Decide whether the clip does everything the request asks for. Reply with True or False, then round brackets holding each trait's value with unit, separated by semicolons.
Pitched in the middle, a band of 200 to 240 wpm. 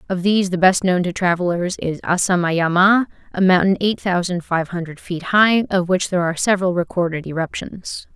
False (180 Hz; 175 wpm)